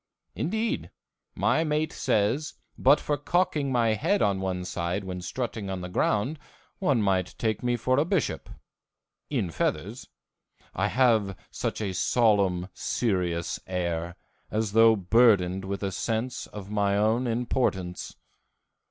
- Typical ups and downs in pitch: Yes, average, 4.9 semitones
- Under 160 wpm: Yes, slow, 135 wpm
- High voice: No, low, 105 Hz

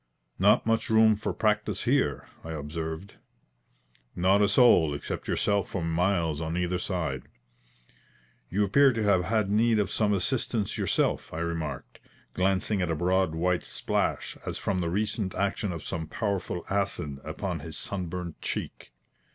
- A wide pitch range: No, average, 3.9 semitones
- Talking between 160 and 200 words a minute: No, average, 150 wpm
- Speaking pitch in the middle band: No, very low, 95 Hz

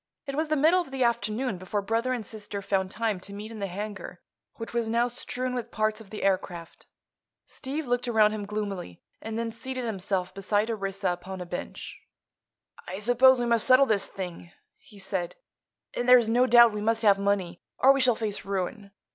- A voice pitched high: Yes, high, 215 Hz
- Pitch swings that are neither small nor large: Yes, average, 3.6 semitones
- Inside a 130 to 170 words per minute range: No, average, 195 wpm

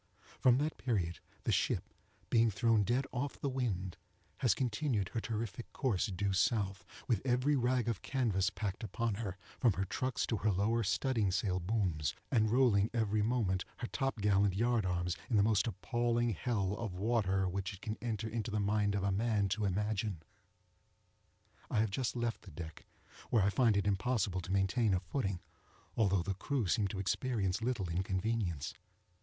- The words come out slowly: No, average, 175 wpm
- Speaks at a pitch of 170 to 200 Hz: No, low, 105 Hz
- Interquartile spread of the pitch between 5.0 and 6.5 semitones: No, average, 3.5 semitones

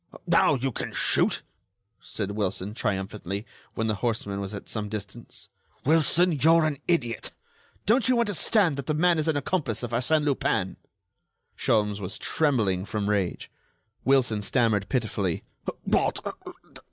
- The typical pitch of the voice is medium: No, low, 115 Hz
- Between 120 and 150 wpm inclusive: Yes, average, 140 wpm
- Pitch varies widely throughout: Yes, wide, 6.9 semitones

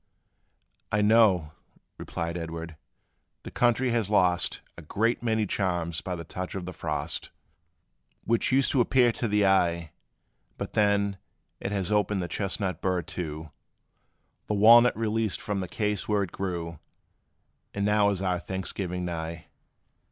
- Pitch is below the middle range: Yes, very low, 95 Hz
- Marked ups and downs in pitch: No, average, 3.4 semitones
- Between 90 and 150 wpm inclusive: Yes, average, 145 wpm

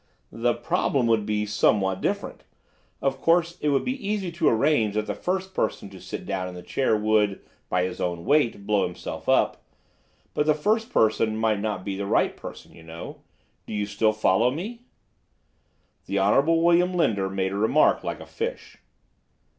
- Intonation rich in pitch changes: Yes, wide, 7.6 semitones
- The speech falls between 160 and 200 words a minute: Yes, average, 180 wpm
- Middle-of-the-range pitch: No, low, 110 Hz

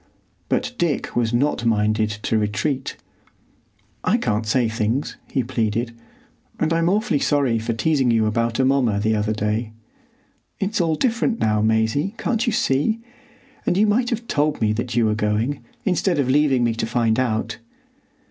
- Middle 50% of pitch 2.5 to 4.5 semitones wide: No, wide, 5.6 semitones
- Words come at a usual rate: Yes, average, 165 wpm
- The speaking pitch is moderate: No, low, 120 Hz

